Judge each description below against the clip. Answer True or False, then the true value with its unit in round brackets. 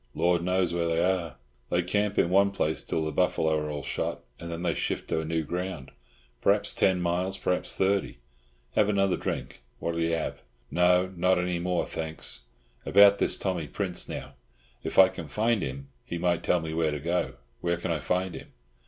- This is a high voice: False (85 Hz)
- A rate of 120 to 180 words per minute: False (195 wpm)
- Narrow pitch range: True (2.3 semitones)